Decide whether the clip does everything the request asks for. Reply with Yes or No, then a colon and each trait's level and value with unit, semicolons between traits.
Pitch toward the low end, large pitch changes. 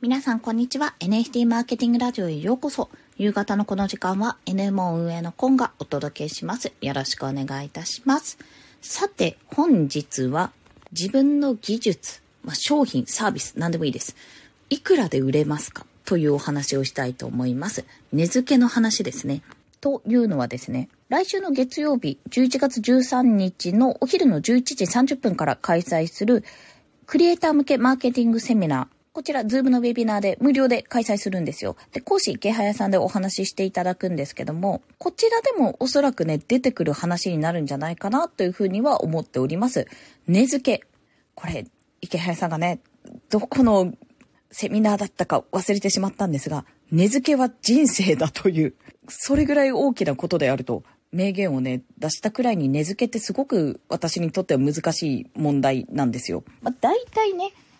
No: high, 205 Hz; wide, 7.6 semitones